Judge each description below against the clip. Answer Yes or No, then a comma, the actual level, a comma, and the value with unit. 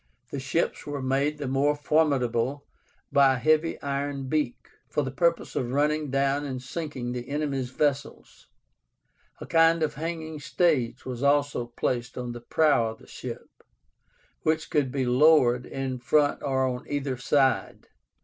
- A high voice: No, medium, 140 Hz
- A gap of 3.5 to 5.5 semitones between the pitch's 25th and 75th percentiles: No, average, 2.8 semitones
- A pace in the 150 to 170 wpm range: Yes, average, 155 wpm